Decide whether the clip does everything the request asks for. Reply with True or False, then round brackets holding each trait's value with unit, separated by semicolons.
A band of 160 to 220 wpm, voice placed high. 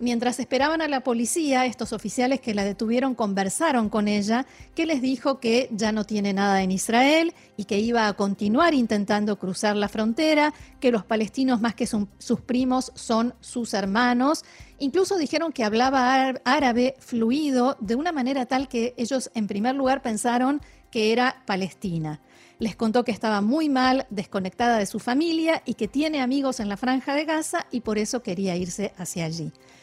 True (175 wpm; 240 Hz)